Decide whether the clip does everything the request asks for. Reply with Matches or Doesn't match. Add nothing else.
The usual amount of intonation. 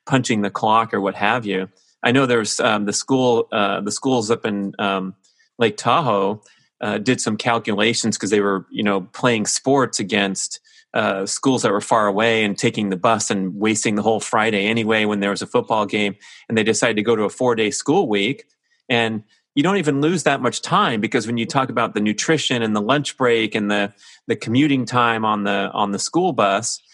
Matches